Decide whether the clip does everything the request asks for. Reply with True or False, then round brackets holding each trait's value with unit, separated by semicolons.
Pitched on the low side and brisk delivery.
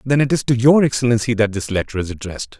True (120 Hz; 255 wpm)